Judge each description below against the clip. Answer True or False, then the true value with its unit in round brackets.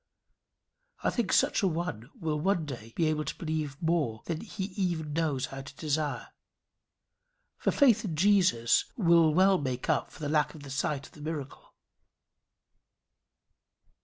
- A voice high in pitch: False (155 Hz)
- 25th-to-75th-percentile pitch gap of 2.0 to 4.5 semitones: True (3.5 semitones)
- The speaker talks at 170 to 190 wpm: False (160 wpm)